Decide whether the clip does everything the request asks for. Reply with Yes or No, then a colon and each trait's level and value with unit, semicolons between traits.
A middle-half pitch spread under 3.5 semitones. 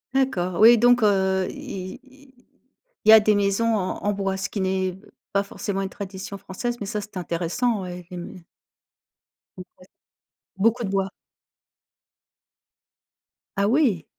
Yes: average, 2.9 semitones